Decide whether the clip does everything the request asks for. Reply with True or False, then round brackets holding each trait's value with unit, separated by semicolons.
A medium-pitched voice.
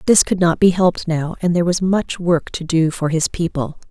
True (170 Hz)